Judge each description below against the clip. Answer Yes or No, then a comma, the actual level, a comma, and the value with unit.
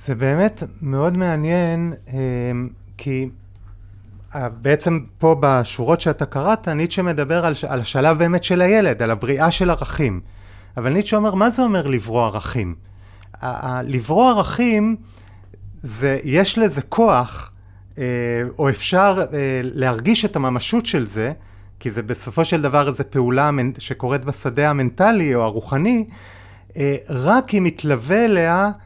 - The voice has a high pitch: No, medium, 140 Hz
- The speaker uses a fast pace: No, average, 125 wpm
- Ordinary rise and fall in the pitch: No, wide, 6.2 semitones